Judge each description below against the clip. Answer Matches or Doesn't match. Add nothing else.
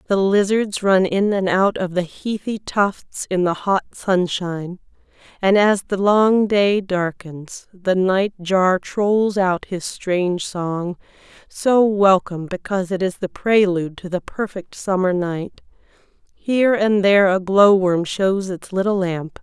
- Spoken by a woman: Matches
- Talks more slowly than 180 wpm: Matches